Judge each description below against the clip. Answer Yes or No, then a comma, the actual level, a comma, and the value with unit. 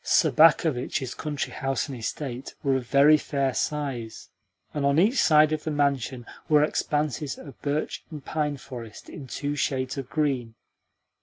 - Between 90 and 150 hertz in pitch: Yes, medium, 140 Hz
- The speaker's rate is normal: Yes, average, 155 wpm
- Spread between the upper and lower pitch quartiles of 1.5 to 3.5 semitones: Yes, narrow, 2.6 semitones